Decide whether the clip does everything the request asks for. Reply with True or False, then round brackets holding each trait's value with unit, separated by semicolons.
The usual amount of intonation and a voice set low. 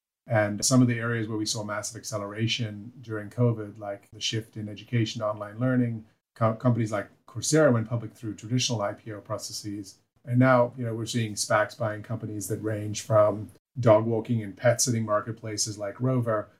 False (2.1 semitones; 110 Hz)